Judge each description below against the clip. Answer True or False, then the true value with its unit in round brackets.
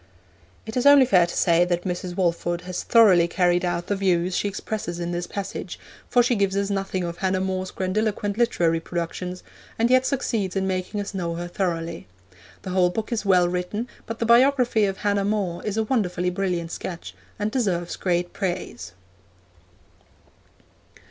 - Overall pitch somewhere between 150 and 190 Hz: True (185 Hz)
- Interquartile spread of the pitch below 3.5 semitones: True (3.0 semitones)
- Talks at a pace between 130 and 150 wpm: False (175 wpm)